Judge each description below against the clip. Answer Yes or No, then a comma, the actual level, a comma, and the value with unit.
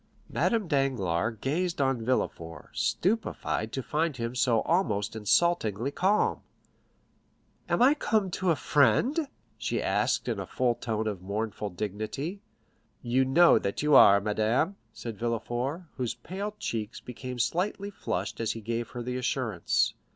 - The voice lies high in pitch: No, low, 125 Hz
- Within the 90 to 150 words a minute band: Yes, average, 145 wpm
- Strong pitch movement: Yes, wide, 7.5 semitones